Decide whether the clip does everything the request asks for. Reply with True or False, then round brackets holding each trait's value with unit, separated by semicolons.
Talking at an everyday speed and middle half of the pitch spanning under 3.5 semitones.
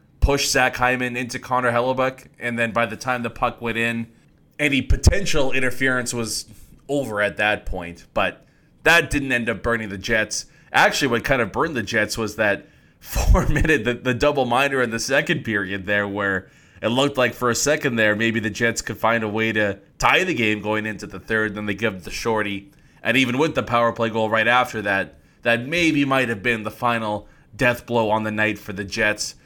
False (210 wpm; 3.0 semitones)